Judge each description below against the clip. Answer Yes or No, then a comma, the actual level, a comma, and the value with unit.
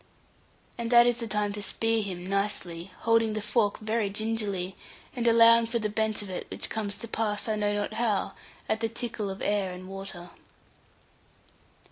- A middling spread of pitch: No, narrow, 2.2 semitones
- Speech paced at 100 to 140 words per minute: No, average, 180 wpm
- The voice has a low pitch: No, high, 215 Hz